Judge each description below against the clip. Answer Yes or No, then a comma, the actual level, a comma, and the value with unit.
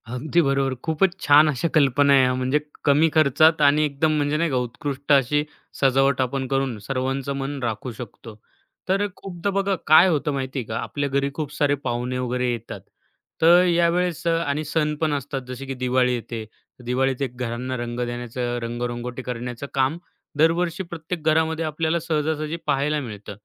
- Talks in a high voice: No, medium, 140 Hz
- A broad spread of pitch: No, average, 3.7 semitones